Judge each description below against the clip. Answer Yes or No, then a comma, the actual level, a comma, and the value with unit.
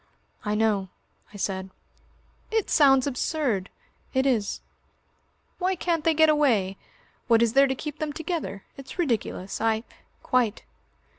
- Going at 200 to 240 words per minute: No, average, 140 wpm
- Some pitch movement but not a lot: No, wide, 6.5 semitones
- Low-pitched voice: No, very high, 260 Hz